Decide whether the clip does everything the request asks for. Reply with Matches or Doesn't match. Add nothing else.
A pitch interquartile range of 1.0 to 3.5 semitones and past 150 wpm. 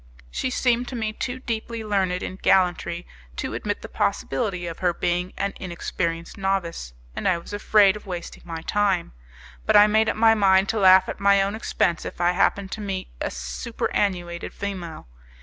Matches